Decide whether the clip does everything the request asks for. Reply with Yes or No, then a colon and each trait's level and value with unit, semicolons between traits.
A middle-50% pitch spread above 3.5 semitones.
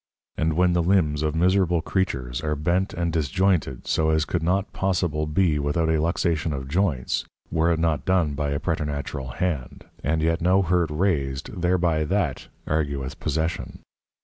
No: average, 3.1 semitones